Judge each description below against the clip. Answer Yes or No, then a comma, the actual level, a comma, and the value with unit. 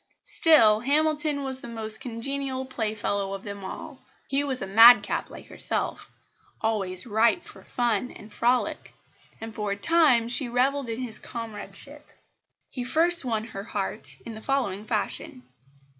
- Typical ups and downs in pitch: Yes, average, 4.2 semitones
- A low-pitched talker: No, high, 235 Hz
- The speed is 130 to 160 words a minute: Yes, average, 150 wpm